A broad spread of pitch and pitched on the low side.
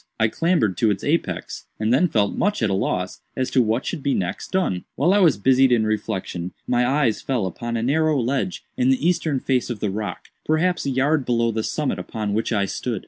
Yes: wide, 5.7 semitones; low, 125 Hz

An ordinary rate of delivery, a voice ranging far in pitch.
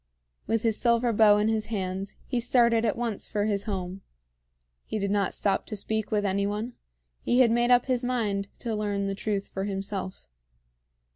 No: average, 190 wpm; average, 2.7 semitones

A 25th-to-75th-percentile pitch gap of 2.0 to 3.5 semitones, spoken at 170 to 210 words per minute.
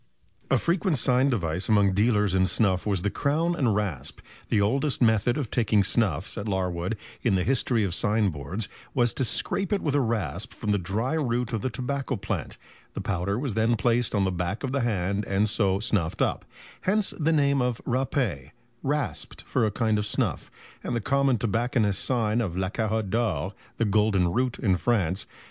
No: average, 4.3 semitones; average, 190 wpm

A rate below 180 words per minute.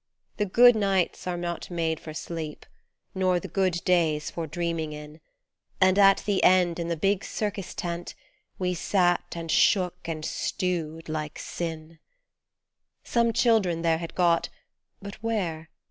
Yes: average, 145 wpm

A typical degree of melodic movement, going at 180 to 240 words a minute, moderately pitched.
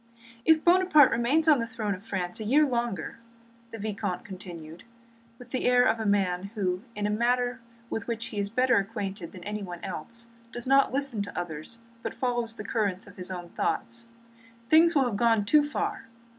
No: average, 3.9 semitones; average, 190 wpm; high, 225 Hz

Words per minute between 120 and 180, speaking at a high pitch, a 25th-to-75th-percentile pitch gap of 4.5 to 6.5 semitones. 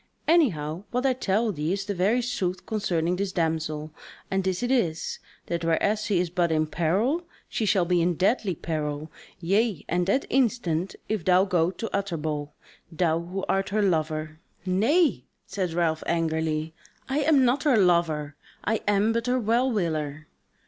No: average, 170 wpm; medium, 180 Hz; average, 5.2 semitones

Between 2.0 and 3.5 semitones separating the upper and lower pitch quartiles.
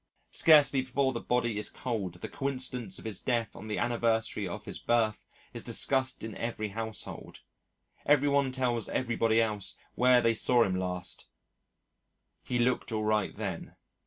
Yes: average, 3.0 semitones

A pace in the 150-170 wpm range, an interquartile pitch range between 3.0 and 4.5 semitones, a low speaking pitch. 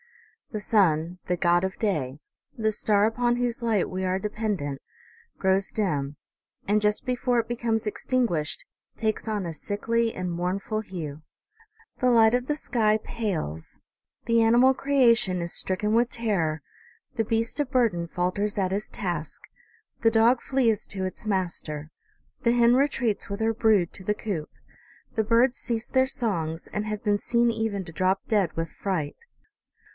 No: average, 160 wpm; average, 4.2 semitones; high, 210 Hz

